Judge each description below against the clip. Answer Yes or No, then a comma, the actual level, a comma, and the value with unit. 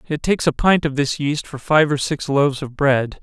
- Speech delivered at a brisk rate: Yes, fast, 260 wpm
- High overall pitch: No, medium, 145 Hz